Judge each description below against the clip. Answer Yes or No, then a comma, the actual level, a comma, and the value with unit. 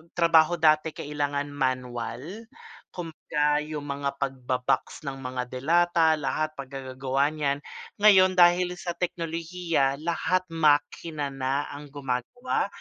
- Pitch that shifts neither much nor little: Yes, average, 3.6 semitones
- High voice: No, medium, 150 Hz